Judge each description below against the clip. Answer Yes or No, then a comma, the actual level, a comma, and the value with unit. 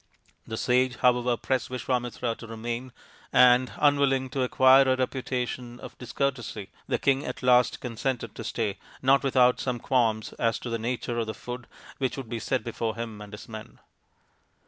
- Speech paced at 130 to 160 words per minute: No, average, 170 wpm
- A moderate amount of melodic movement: No, narrow, 2.1 semitones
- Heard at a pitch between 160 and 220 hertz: No, low, 125 Hz